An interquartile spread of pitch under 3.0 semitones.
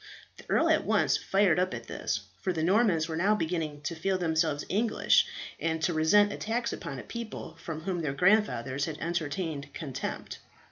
No: average, 3.7 semitones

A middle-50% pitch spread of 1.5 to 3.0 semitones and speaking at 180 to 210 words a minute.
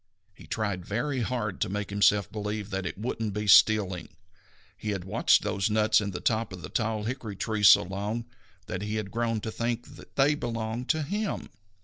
Yes: narrow, 2.5 semitones; average, 200 wpm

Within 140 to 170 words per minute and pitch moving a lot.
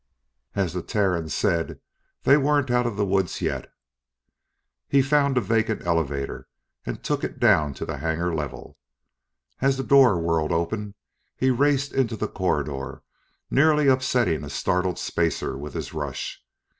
Yes: average, 150 wpm; wide, 8.0 semitones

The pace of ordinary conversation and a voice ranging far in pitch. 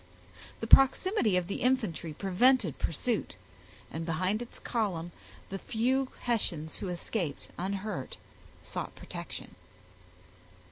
No: slow, 105 wpm; wide, 5.9 semitones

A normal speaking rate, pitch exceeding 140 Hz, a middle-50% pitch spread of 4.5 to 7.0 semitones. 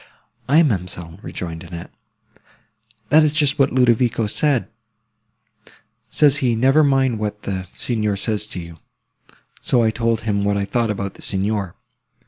No: average, 145 wpm; low, 110 Hz; average, 4.9 semitones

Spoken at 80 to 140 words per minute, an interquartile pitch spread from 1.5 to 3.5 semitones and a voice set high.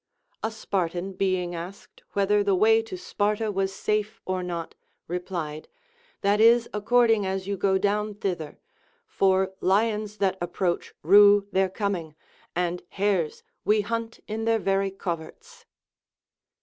Yes: slow, 135 wpm; narrow, 2.4 semitones; high, 195 Hz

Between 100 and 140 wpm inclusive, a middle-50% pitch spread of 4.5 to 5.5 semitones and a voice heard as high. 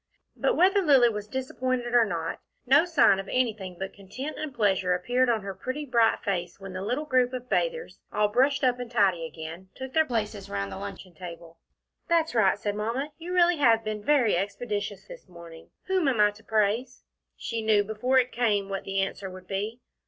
No: average, 200 wpm; average, 4.9 semitones; high, 220 Hz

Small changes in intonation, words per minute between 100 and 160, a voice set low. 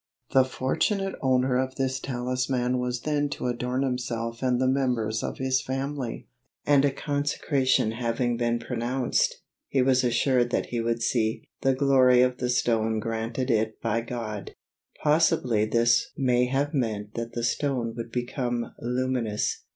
Yes: narrow, 2.1 semitones; average, 150 wpm; low, 125 Hz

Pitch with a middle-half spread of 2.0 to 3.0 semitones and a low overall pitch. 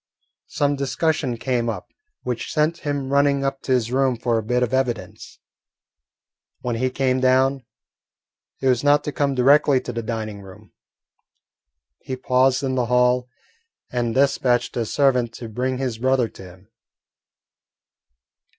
Yes: narrow, 2.4 semitones; low, 130 Hz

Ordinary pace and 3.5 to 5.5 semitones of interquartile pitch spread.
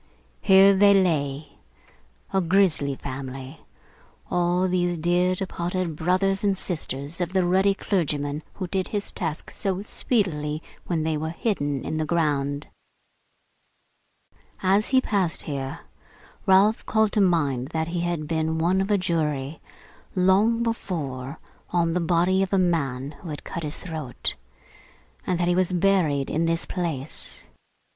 Yes: average, 145 wpm; average, 4.0 semitones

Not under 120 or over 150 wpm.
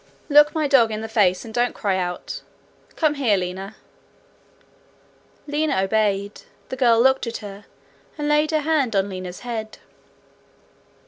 Yes: average, 145 wpm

